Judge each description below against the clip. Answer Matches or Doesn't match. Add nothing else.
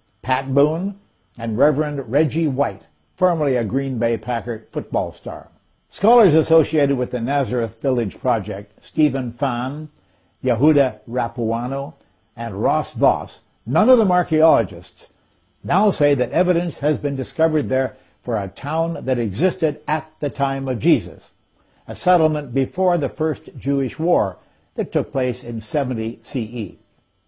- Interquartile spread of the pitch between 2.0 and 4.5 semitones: Doesn't match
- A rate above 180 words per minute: Doesn't match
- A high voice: Doesn't match